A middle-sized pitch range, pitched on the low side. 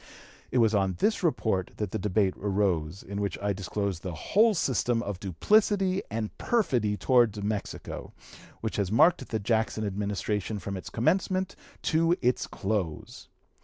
Yes: average, 4.4 semitones; low, 105 Hz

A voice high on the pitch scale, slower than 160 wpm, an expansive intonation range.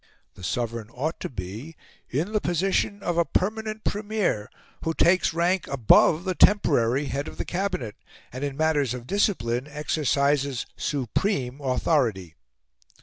No: medium, 145 Hz; average, 140 wpm; wide, 6.7 semitones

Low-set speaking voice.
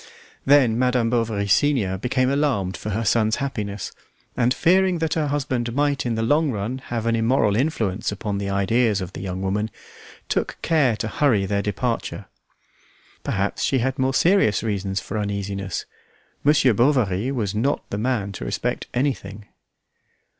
Yes: low, 115 Hz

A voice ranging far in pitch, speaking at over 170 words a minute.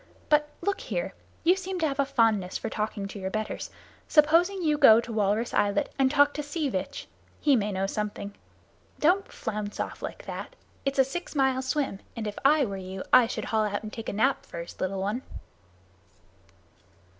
Yes: wide, 6.4 semitones; average, 190 wpm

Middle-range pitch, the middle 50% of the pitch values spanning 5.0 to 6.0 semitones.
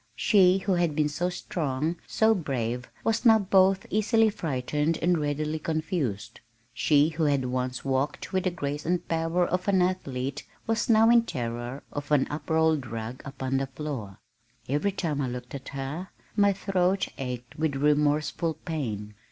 Yes: medium, 150 Hz; average, 5.3 semitones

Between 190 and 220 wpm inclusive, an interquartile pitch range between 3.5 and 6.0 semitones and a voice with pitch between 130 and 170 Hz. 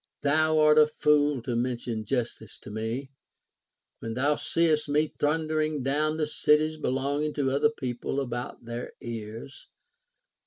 No: average, 145 wpm; average, 4.0 semitones; medium, 140 Hz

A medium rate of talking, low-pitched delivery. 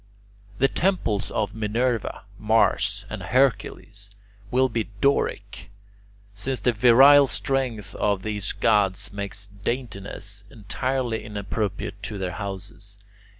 No: slow, 110 wpm; low, 105 Hz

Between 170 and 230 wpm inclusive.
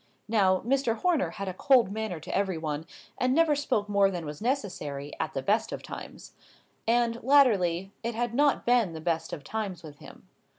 Yes: average, 195 wpm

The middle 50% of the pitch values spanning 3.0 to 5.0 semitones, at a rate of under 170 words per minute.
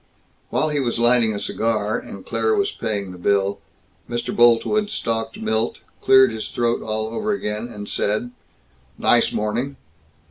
No: narrow, 2.4 semitones; average, 150 wpm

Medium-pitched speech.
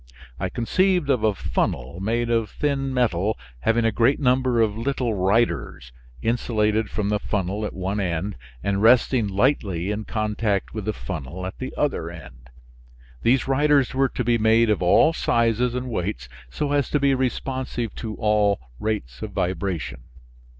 No: low, 110 Hz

